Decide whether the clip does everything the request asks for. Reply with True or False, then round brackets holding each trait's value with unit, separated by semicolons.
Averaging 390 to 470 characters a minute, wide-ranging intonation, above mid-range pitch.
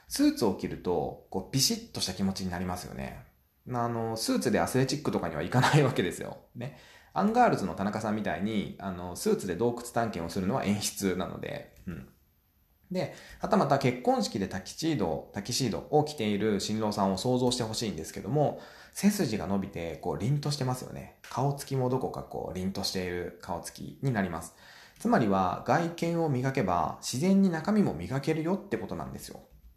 False (405 characters per minute; 7.4 semitones; 120 Hz)